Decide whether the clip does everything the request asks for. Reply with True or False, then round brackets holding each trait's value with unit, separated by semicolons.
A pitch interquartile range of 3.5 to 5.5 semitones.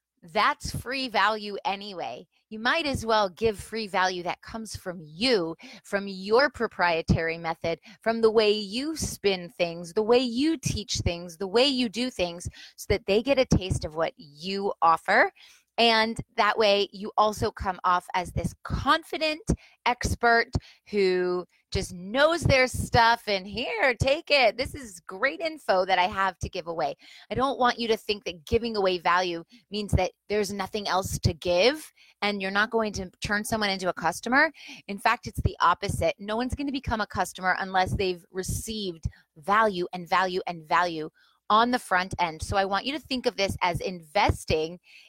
True (4.5 semitones)